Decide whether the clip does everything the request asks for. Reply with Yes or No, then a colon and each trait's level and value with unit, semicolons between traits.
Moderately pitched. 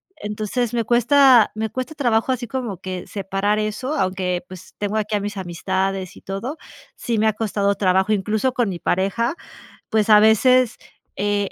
No: high, 210 Hz